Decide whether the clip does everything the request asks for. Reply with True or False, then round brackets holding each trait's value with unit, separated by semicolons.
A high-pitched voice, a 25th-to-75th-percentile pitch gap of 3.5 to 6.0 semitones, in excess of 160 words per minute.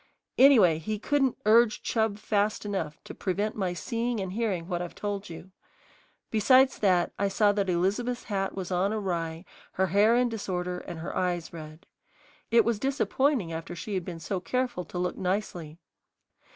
True (195 Hz; 3.9 semitones; 170 wpm)